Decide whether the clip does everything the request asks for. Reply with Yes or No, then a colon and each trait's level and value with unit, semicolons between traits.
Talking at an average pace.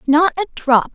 Yes: average, 190 wpm